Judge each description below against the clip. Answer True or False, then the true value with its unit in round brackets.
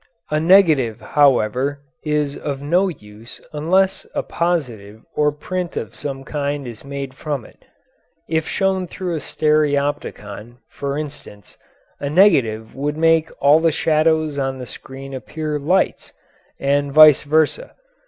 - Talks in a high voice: False (145 Hz)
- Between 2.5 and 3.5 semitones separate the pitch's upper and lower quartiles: True (3.0 semitones)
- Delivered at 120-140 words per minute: True (135 wpm)